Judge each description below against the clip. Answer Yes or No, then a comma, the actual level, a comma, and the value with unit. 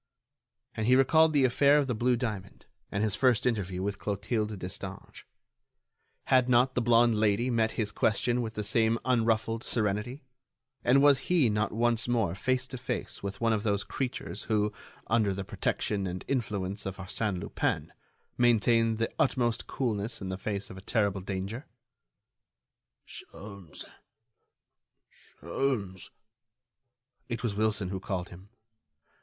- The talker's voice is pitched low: Yes, low, 110 Hz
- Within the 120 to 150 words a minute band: Yes, average, 145 wpm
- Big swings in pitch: No, average, 3.4 semitones